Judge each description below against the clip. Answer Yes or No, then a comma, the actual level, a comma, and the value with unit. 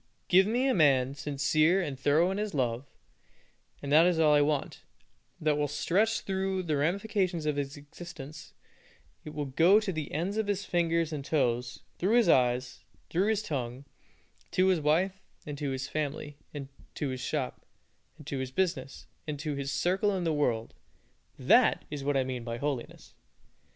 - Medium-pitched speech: Yes, medium, 150 Hz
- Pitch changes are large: No, average, 4.8 semitones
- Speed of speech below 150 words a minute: No, average, 185 wpm